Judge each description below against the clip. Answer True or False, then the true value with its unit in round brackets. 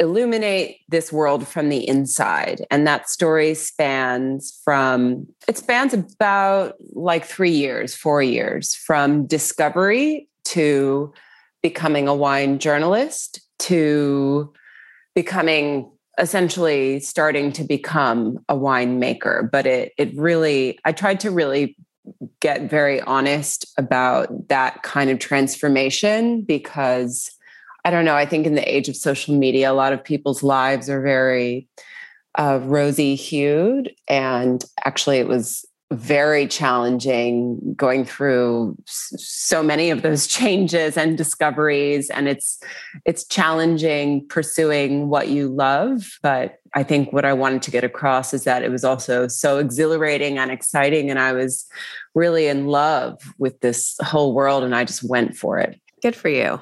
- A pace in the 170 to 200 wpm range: False (140 wpm)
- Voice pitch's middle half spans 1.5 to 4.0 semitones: True (2.9 semitones)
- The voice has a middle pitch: True (145 Hz)